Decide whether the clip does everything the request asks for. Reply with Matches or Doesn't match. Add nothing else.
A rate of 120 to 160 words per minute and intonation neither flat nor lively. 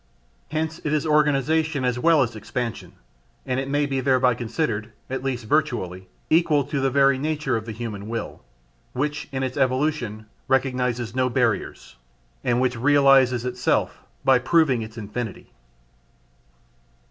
Matches